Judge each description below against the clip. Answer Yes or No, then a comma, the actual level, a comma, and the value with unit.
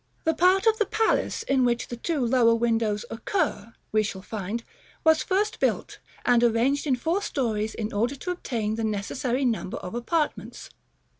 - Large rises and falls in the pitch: Yes, wide, 6.2 semitones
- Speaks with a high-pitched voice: Yes, high, 240 Hz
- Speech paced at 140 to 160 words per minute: No, average, 170 wpm